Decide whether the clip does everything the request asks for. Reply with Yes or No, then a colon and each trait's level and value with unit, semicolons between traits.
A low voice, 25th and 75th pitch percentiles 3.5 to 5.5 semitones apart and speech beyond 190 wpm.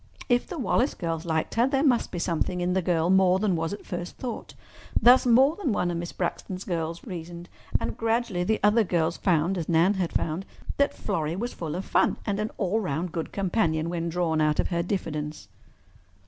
No: medium, 180 Hz; average, 4.3 semitones; fast, 205 wpm